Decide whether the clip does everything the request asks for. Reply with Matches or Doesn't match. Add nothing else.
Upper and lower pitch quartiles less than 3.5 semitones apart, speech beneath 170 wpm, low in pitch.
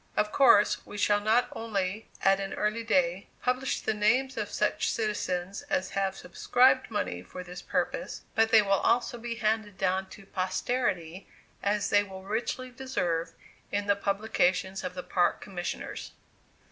Doesn't match